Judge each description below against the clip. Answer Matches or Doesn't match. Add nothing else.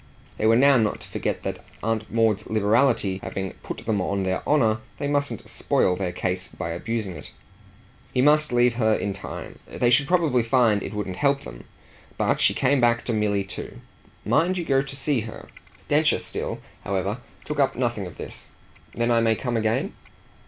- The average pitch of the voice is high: Doesn't match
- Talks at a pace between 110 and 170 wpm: Doesn't match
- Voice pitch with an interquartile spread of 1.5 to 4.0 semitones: Doesn't match